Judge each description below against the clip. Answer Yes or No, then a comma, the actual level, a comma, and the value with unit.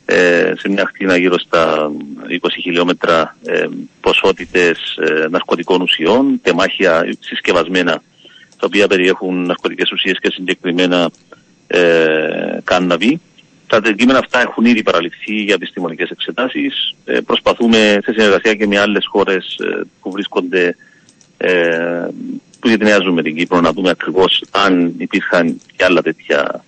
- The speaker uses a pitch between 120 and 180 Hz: No, very low, 90 Hz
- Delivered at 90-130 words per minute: Yes, average, 125 wpm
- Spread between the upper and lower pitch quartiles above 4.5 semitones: No, average, 3.5 semitones